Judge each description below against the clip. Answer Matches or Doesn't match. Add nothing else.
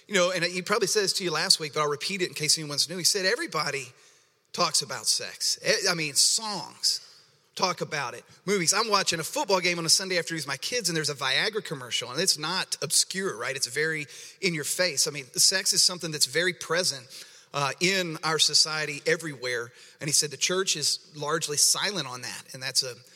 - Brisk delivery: Matches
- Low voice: Doesn't match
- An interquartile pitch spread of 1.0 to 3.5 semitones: Doesn't match